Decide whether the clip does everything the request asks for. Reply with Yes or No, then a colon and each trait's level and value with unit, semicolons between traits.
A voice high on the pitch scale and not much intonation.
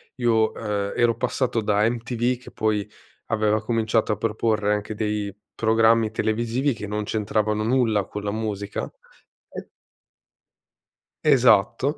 No: low, 110 Hz; narrow, 1.9 semitones